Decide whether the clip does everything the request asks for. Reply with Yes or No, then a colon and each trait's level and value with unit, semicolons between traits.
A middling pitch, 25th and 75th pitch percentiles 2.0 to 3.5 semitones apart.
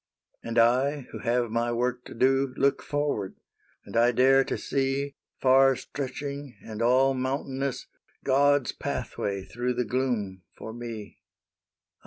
No: low, 130 Hz; narrow, 2.5 semitones